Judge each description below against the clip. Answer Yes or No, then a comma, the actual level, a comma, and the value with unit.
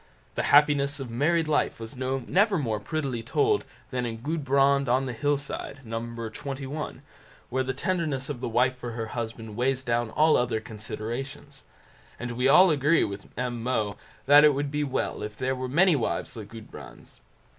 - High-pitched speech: No, low, 130 Hz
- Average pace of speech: Yes, average, 175 wpm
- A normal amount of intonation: Yes, average, 3.7 semitones